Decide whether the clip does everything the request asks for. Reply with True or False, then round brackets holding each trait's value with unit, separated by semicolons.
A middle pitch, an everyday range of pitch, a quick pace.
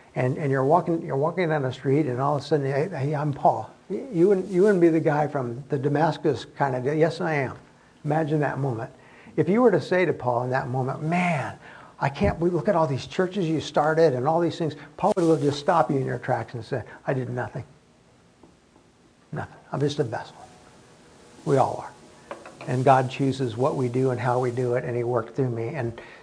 True (145 Hz; 4.0 semitones; 230 wpm)